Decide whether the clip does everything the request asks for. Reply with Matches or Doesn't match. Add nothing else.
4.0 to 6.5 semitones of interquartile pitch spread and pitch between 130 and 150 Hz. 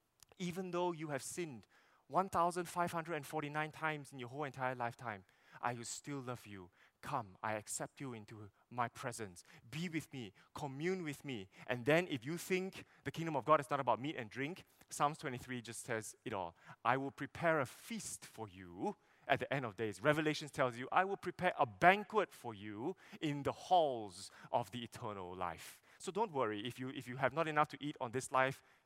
Matches